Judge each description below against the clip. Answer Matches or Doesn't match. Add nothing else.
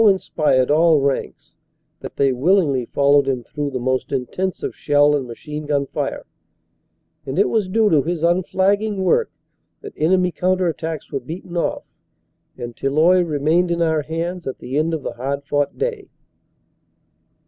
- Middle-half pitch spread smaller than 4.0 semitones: Doesn't match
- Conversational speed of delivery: Matches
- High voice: Doesn't match